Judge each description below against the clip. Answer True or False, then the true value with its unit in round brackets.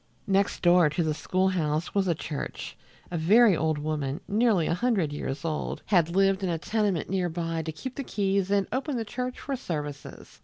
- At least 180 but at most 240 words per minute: True (200 wpm)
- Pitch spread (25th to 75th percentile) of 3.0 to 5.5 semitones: True (4.3 semitones)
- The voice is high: False (180 Hz)